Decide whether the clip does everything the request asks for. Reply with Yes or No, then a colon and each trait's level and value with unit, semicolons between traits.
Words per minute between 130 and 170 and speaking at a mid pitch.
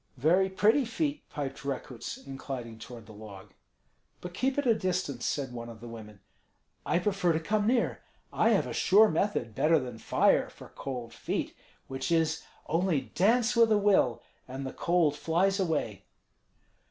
Yes: average, 165 wpm; medium, 160 Hz